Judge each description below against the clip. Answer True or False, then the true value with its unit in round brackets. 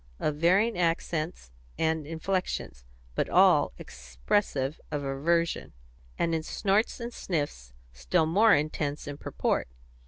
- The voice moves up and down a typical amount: True (3.9 semitones)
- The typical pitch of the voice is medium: True (160 Hz)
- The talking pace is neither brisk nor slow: False (120 wpm)